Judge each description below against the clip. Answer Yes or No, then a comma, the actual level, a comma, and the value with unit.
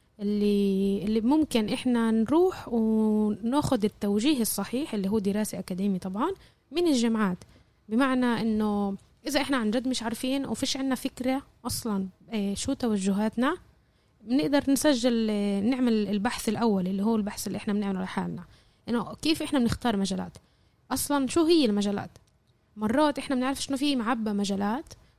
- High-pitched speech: Yes, high, 225 Hz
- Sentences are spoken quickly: Yes, fast, 140 wpm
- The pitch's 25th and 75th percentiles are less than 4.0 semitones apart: No, average, 4.6 semitones